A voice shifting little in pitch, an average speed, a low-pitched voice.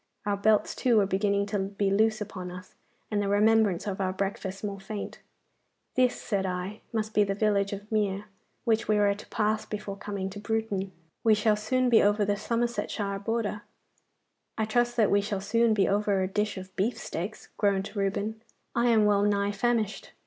No: narrow, 1.7 semitones; average, 185 wpm; high, 205 Hz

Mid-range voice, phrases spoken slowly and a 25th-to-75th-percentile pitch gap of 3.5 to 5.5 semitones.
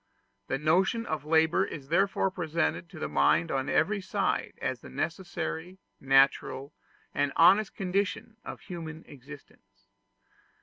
Yes: medium, 160 Hz; slow, 130 wpm; average, 4.7 semitones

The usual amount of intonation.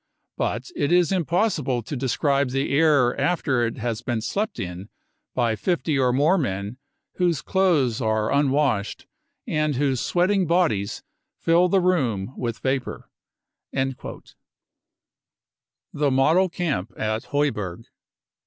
No: wide, 6.0 semitones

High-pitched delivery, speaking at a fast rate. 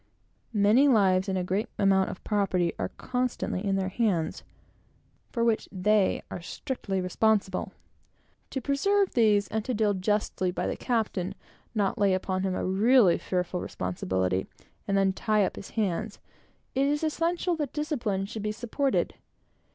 No: high, 205 Hz; average, 160 wpm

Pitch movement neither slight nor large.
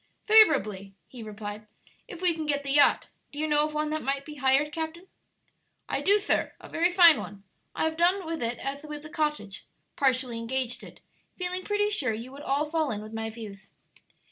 No: wide, 5.7 semitones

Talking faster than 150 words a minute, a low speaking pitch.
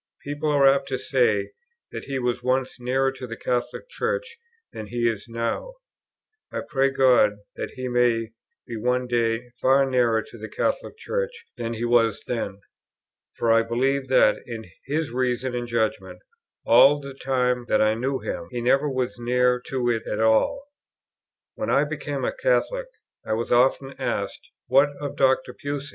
Yes: average, 170 wpm; low, 125 Hz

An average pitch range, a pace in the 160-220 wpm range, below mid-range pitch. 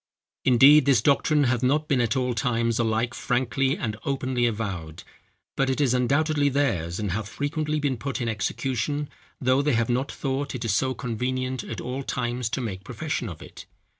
Yes: average, 3.3 semitones; average, 180 wpm; low, 125 Hz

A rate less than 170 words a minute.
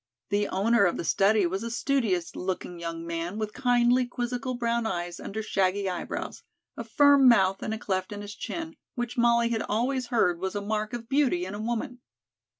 No: average, 195 wpm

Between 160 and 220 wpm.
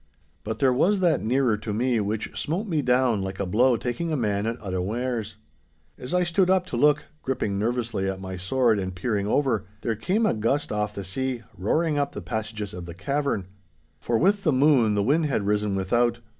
Yes: fast, 205 wpm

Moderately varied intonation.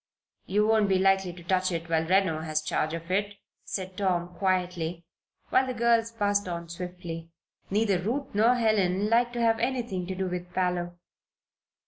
Yes: average, 3.6 semitones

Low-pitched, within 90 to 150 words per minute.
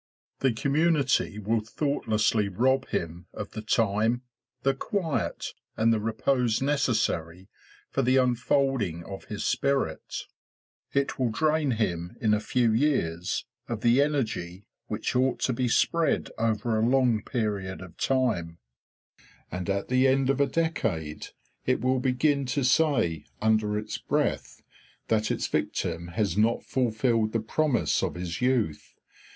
Yes: low, 115 Hz; average, 140 wpm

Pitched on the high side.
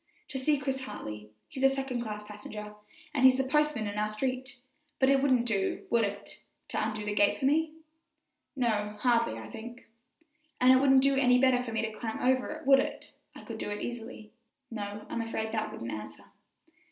Yes: high, 240 Hz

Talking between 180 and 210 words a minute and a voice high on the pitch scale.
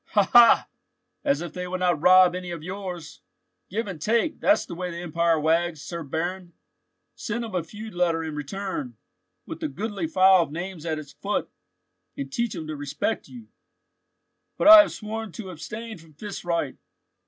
No: average, 185 wpm; medium, 180 Hz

